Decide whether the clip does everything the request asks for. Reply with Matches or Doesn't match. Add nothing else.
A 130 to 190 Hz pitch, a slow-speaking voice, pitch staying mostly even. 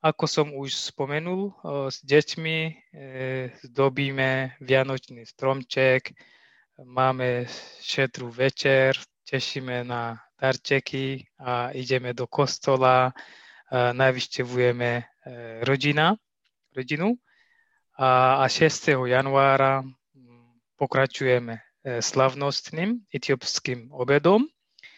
Matches